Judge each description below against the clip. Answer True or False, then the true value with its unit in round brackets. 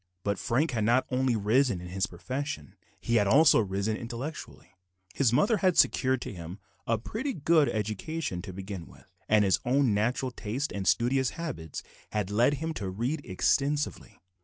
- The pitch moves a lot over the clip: True (5.8 semitones)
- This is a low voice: True (120 Hz)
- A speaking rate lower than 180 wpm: True (170 wpm)